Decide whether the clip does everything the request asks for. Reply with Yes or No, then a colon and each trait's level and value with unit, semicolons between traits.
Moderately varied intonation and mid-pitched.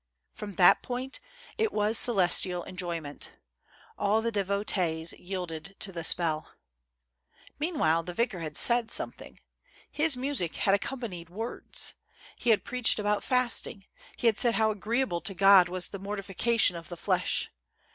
No: average, 4.7 semitones; high, 200 Hz